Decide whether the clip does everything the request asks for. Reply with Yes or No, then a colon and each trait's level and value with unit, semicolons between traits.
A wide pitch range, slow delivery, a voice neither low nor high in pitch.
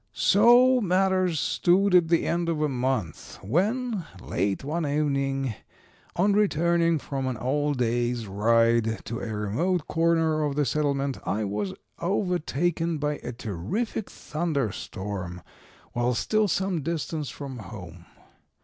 Yes: wide, 6.8 semitones; slow, 130 wpm; medium, 145 Hz